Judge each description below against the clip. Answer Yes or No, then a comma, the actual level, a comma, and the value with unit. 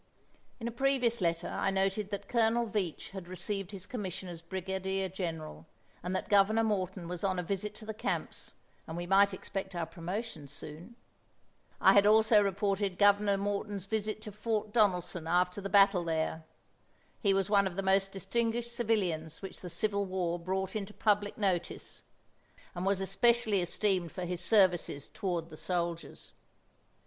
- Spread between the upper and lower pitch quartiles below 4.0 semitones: Yes, average, 2.8 semitones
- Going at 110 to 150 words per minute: No, average, 165 wpm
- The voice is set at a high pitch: Yes, high, 195 Hz